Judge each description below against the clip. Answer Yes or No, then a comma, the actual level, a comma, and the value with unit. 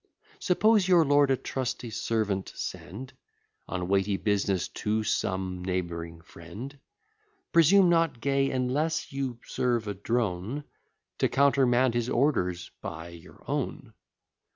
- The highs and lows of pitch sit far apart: Yes, wide, 6.6 semitones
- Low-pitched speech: Yes, low, 120 Hz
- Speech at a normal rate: No, slow, 120 wpm